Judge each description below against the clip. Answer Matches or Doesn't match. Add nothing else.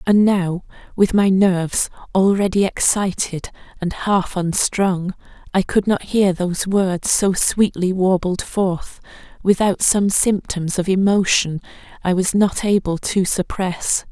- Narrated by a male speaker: Doesn't match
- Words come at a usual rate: Doesn't match